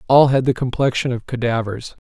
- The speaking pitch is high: No, low, 125 Hz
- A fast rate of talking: No, average, 175 wpm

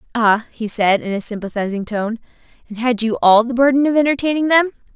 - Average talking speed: Yes, average, 195 wpm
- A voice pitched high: Yes, high, 235 Hz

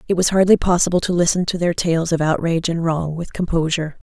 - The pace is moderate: No, fast, 220 wpm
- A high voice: No, medium, 170 Hz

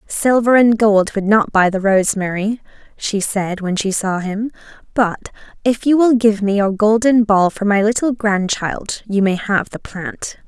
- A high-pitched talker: Yes, high, 210 Hz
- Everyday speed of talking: Yes, average, 185 wpm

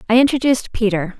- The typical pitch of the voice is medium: No, high, 225 Hz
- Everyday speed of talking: Yes, average, 150 wpm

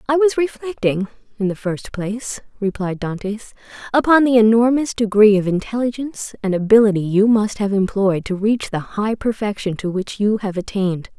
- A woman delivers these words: Yes, female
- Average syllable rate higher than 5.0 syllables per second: Yes, 5.2 syllables/s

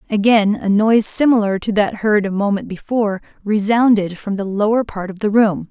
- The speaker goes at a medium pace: Yes, average, 190 wpm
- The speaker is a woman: Yes, female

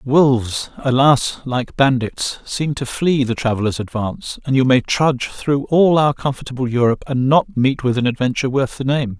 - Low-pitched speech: Yes, low, 130 Hz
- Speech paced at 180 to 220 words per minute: Yes, average, 185 wpm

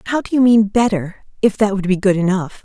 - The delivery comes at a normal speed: No, fast, 225 wpm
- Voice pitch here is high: Yes, high, 205 Hz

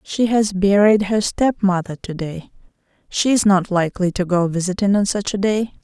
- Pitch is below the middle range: No, high, 195 Hz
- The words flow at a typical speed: Yes, average, 185 wpm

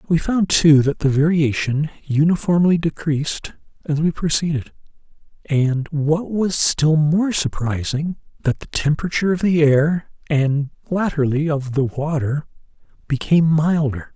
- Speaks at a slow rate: Yes, slow, 125 wpm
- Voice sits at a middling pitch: Yes, medium, 155 Hz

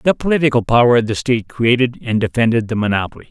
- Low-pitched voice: Yes, low, 120 Hz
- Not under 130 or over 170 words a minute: No, average, 200 wpm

